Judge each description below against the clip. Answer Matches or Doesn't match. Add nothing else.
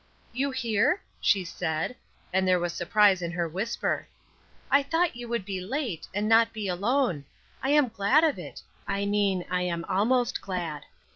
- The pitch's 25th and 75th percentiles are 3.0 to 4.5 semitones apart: Doesn't match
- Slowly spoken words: Doesn't match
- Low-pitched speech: Doesn't match